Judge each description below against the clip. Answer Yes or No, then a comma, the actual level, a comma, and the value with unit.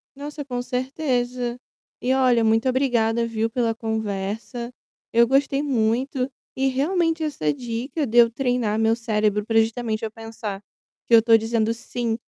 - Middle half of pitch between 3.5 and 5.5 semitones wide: No, narrow, 2.6 semitones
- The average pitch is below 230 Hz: No, high, 235 Hz